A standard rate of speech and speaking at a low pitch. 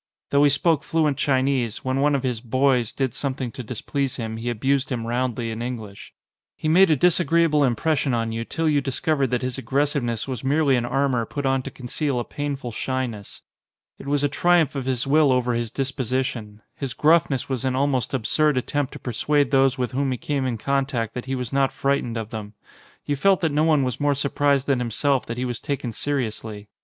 No: fast, 210 wpm; low, 130 Hz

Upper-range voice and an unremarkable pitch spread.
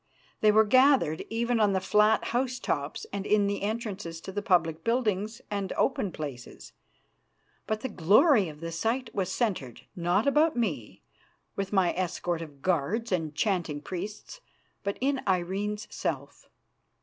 Yes: high, 200 Hz; average, 4.5 semitones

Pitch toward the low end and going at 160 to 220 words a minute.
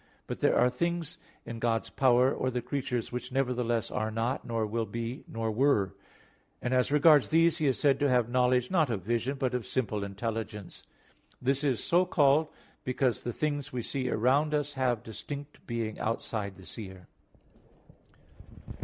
Yes: low, 125 Hz; average, 170 wpm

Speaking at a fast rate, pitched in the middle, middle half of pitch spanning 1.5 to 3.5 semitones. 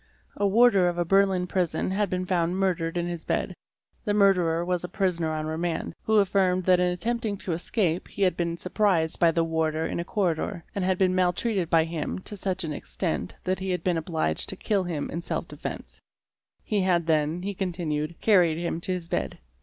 Yes: fast, 210 wpm; medium, 180 Hz; narrow, 2.6 semitones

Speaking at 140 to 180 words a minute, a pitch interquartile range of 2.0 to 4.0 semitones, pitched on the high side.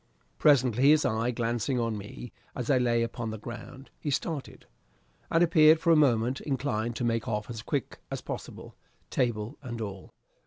No: average, 170 wpm; average, 3.7 semitones; low, 120 Hz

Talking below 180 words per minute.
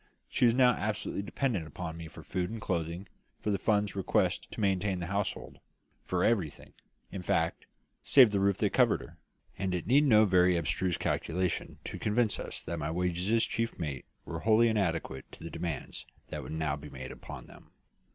No: average, 190 wpm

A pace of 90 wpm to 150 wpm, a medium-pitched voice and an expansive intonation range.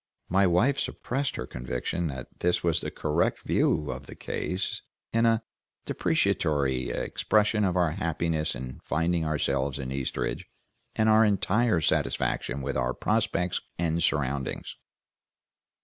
No: slow, 135 wpm; very low, 85 Hz; wide, 5.9 semitones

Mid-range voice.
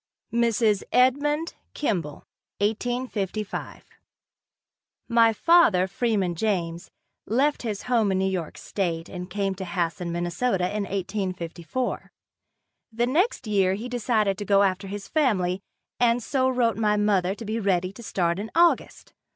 No: high, 205 Hz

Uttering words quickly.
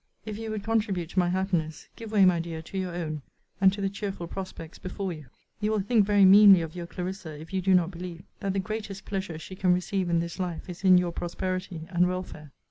Yes: fast, 235 wpm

